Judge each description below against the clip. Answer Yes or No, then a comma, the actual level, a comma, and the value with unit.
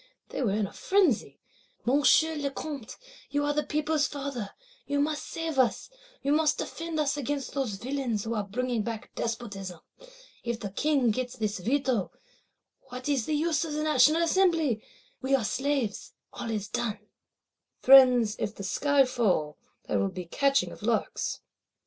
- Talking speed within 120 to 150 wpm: No, average, 160 wpm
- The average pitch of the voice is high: Yes, very high, 260 Hz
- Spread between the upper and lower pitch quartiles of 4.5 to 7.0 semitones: Yes, average, 4.9 semitones